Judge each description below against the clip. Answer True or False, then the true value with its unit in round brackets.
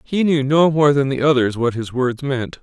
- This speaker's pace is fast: True (250 wpm)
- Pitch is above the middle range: False (135 Hz)